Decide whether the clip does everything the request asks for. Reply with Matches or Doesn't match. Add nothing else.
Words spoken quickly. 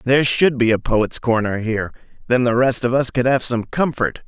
Matches